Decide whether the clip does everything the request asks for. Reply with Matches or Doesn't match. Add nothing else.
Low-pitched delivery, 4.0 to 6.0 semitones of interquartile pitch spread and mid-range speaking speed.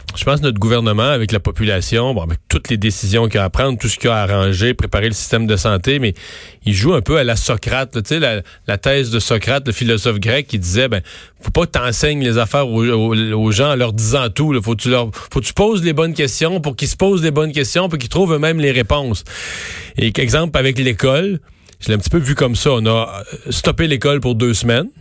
Doesn't match